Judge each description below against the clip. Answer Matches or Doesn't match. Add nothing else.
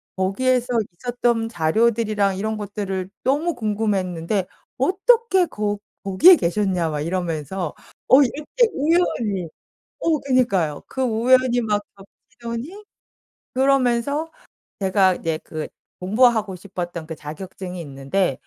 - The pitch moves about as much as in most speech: Doesn't match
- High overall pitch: Matches